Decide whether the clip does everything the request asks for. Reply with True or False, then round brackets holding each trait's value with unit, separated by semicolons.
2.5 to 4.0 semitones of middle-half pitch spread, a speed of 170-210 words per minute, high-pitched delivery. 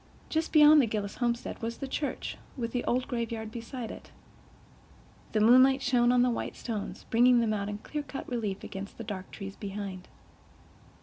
True (3.2 semitones; 180 wpm; 235 Hz)